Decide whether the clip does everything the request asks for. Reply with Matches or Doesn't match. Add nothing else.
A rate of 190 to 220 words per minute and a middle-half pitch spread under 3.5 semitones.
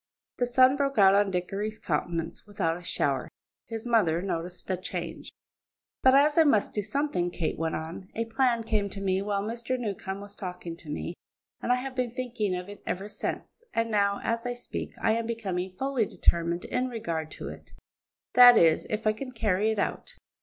Doesn't match